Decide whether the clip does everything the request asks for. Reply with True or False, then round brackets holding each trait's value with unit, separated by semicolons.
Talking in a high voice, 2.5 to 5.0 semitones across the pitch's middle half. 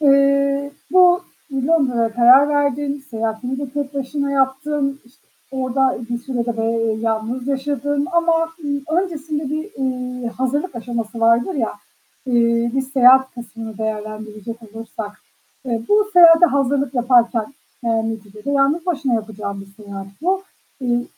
True (260 Hz; 3.7 semitones)